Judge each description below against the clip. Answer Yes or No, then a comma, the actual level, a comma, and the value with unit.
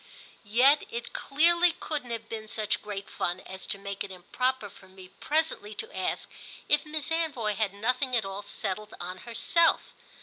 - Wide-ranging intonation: Yes, wide, 6.4 semitones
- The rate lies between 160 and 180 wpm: Yes, average, 170 wpm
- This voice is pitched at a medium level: No, high, 220 Hz